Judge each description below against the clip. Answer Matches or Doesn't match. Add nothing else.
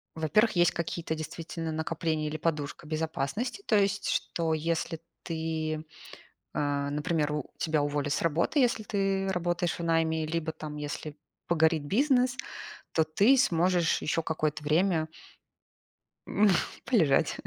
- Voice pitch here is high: Doesn't match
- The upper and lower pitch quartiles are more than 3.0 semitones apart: Doesn't match